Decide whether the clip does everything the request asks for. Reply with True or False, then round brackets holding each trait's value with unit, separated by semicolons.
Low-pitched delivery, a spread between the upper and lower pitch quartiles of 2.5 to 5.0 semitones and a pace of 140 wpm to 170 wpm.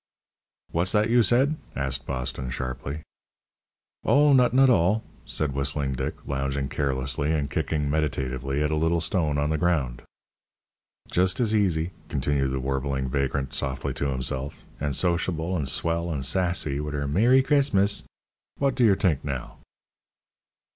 False (75 Hz; 5.4 semitones; 150 wpm)